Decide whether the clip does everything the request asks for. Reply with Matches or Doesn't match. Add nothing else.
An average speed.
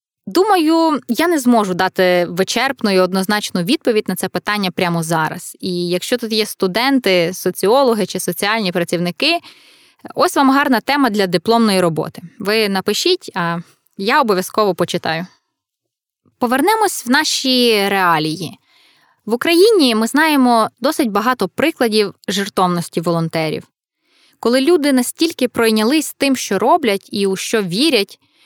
Matches